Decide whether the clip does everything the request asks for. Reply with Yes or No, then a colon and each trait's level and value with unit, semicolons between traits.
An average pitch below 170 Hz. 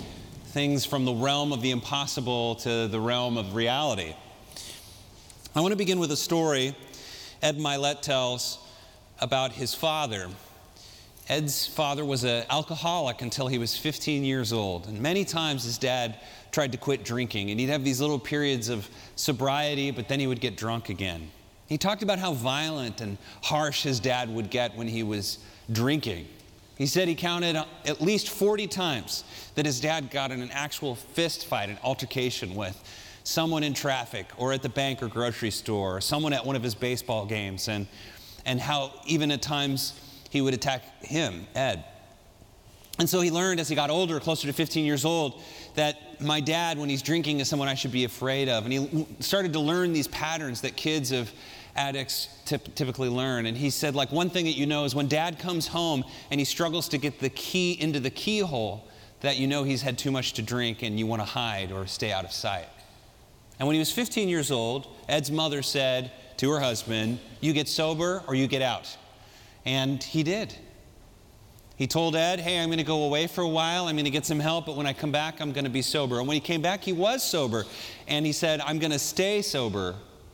Yes: low, 135 Hz